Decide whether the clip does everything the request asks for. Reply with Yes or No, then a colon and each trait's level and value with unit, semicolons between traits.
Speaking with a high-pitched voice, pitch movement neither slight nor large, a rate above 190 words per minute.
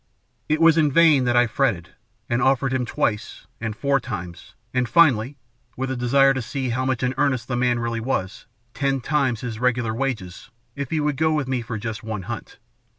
No: low, 125 Hz; average, 3.0 semitones; fast, 205 wpm